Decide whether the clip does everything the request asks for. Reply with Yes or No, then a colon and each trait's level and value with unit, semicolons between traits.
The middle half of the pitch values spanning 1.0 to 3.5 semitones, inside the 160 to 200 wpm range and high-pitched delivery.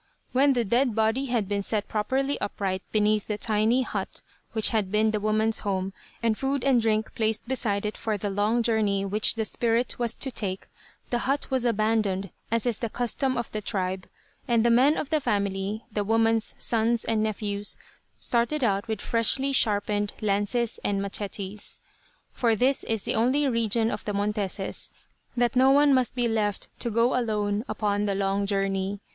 Yes: average, 2.7 semitones; average, 180 wpm; high, 220 Hz